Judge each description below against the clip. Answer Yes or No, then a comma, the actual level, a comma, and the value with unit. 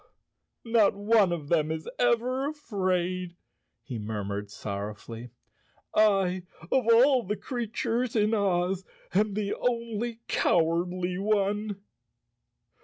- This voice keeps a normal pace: No, slow, 100 wpm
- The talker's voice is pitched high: Yes, high, 195 Hz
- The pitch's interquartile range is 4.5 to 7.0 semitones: Yes, average, 4.8 semitones